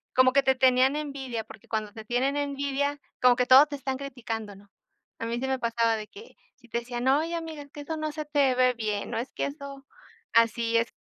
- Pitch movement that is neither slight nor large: Yes, average, 3.4 semitones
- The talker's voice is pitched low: No, very high, 255 Hz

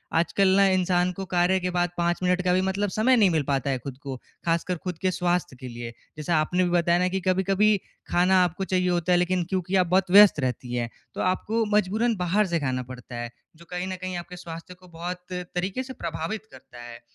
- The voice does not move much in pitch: Yes, narrow, 2.2 semitones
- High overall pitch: No, medium, 180 Hz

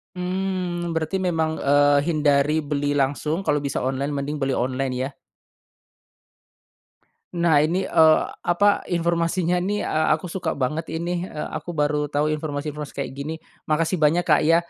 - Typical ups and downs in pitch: Yes, average, 3.1 semitones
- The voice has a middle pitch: Yes, medium, 155 Hz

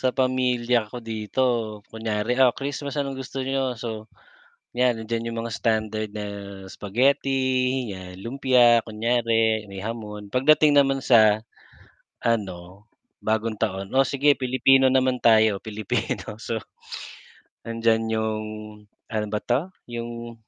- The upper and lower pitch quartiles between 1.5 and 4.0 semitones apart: Yes, average, 3.0 semitones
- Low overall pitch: Yes, low, 115 Hz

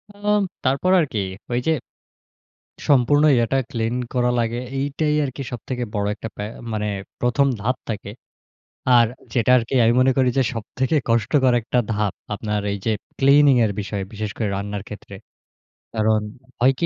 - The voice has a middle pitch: No, low, 120 Hz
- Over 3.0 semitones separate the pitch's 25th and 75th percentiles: Yes, average, 3.6 semitones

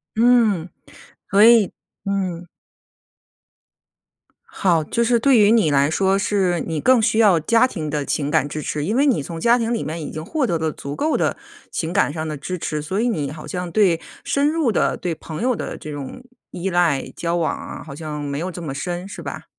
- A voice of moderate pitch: Yes, medium, 175 Hz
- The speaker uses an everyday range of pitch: No, wide, 6.4 semitones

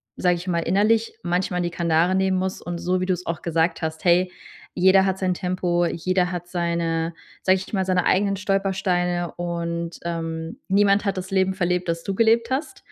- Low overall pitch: No, medium, 180 Hz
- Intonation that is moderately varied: No, narrow, 1.9 semitones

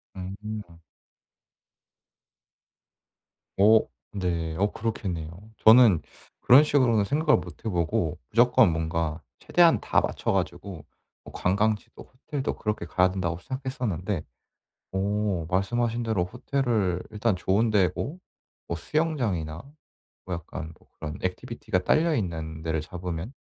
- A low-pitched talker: Yes, low, 100 Hz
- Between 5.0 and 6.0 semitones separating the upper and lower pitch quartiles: Yes, average, 5.3 semitones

